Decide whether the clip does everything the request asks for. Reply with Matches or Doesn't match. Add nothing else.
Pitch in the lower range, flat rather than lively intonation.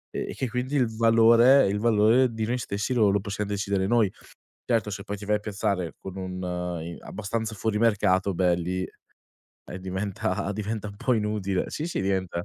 Doesn't match